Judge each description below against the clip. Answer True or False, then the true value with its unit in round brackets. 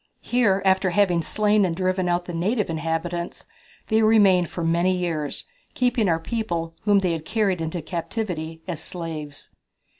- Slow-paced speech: False (155 wpm)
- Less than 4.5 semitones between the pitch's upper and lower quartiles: True (3.7 semitones)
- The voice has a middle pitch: True (180 Hz)